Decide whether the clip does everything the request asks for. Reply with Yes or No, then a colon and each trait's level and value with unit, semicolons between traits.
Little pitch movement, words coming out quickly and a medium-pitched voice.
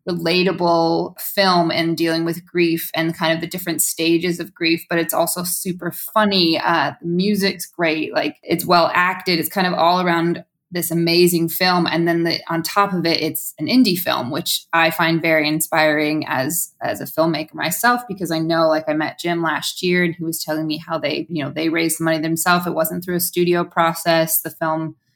Yes: narrow, 1.4 semitones; fast, 210 wpm; medium, 165 Hz